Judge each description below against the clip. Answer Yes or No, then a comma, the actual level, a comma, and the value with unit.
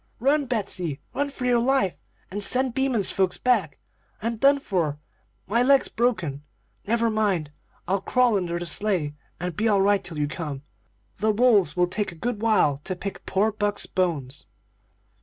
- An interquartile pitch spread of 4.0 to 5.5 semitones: Yes, average, 5.2 semitones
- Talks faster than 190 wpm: No, average, 170 wpm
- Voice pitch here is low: No, high, 205 Hz